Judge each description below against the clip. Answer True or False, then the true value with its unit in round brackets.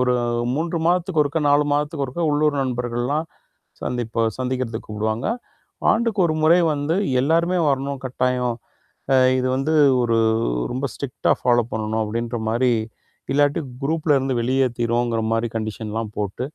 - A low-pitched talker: True (130 Hz)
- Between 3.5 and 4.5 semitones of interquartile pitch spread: True (3.9 semitones)